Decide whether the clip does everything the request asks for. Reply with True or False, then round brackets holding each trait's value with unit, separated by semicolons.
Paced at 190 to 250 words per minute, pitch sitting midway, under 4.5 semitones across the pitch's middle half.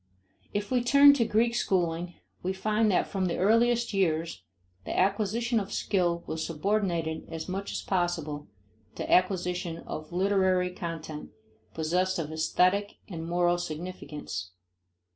False (135 wpm; 180 Hz; 3.5 semitones)